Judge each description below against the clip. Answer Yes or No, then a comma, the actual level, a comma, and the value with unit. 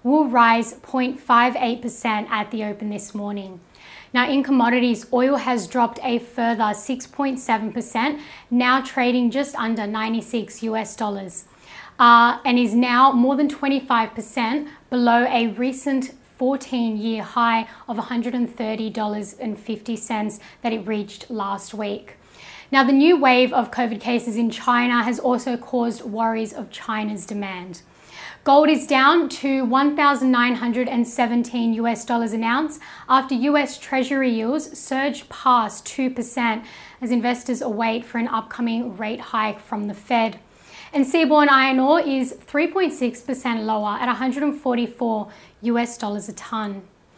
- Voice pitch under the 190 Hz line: No, high, 240 Hz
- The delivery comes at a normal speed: No, slow, 125 wpm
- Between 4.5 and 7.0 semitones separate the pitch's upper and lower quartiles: No, average, 2.8 semitones